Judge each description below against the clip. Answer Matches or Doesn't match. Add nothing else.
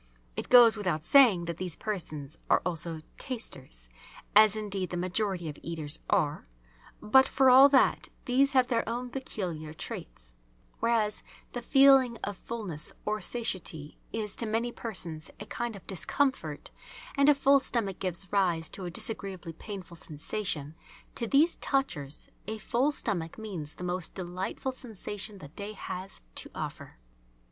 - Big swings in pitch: Matches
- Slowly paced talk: Doesn't match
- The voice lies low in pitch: Doesn't match